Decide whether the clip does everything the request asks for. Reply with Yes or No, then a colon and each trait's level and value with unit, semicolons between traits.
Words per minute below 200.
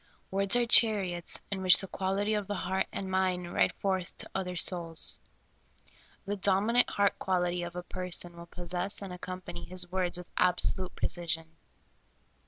Yes: average, 160 wpm